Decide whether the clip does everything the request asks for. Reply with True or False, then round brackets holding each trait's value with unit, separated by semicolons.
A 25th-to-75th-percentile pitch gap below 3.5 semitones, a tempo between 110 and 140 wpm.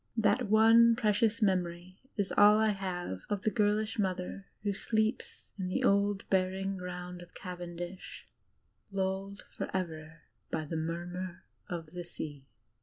True (2.9 semitones; 135 wpm)